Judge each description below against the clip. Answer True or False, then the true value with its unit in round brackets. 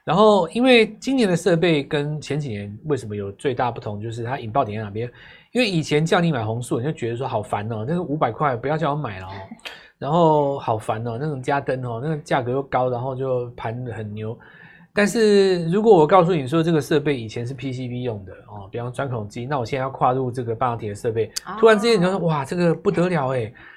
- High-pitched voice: False (140 Hz)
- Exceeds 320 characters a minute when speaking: True (345 characters per minute)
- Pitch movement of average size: False (6.0 semitones)